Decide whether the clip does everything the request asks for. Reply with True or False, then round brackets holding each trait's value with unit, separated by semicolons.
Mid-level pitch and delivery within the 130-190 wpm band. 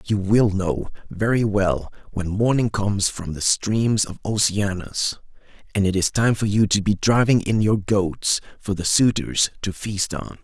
False (100 Hz; 180 wpm)